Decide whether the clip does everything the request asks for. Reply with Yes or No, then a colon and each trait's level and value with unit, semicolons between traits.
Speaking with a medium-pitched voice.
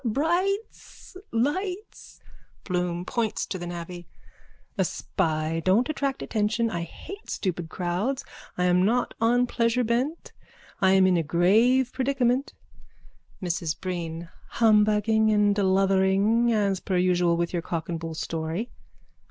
No: high, 200 Hz